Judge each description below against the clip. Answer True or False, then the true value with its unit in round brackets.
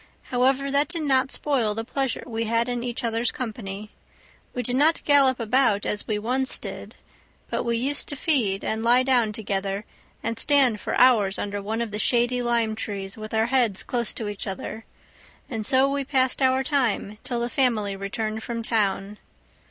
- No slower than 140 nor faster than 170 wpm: False (185 wpm)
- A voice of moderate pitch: False (235 Hz)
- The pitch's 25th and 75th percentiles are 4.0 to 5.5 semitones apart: False (3.5 semitones)